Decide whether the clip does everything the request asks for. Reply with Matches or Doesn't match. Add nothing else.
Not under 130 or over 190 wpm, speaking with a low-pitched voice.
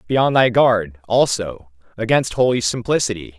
Matches